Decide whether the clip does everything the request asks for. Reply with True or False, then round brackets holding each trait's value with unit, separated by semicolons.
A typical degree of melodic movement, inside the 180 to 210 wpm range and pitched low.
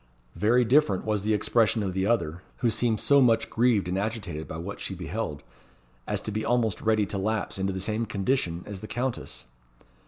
True (3.2 semitones; 195 wpm; 105 Hz)